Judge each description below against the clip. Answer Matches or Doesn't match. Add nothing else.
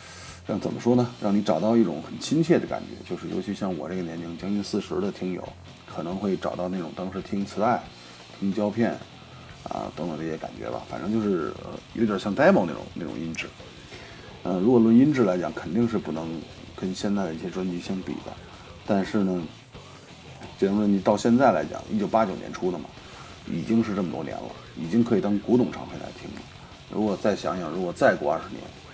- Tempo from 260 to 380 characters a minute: Matches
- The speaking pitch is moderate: Doesn't match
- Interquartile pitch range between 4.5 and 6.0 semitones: Doesn't match